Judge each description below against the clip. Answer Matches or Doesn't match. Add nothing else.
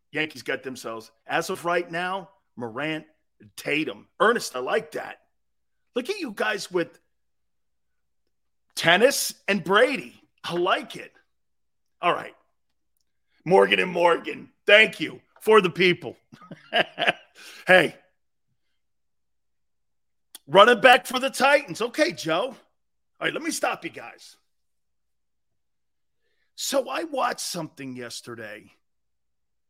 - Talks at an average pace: Doesn't match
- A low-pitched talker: Doesn't match